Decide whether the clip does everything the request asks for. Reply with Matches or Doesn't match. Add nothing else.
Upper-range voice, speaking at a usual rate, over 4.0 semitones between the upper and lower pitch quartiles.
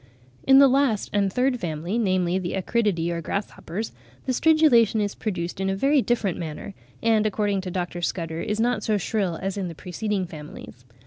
Matches